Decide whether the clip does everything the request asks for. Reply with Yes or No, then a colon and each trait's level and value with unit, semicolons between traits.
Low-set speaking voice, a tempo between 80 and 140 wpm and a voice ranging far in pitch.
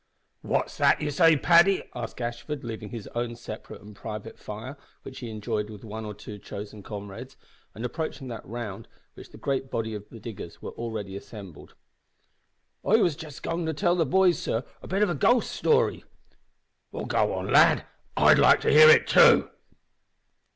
No: low, 120 Hz; average, 180 wpm; wide, 7.0 semitones